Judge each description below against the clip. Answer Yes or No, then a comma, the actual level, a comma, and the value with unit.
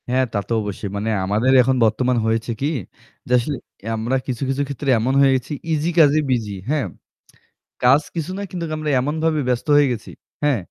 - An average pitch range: Yes, average, 4.1 semitones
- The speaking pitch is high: No, low, 130 Hz